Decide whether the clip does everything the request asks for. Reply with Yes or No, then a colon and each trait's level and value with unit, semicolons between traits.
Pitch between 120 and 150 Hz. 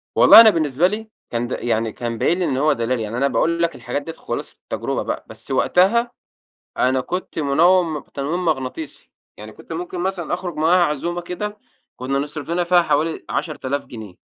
No: medium, 160 Hz